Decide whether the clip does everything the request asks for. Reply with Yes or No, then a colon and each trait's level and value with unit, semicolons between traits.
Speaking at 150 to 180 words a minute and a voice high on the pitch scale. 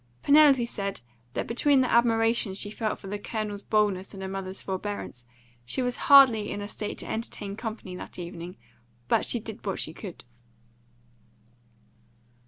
Yes: average, 160 wpm; high, 210 Hz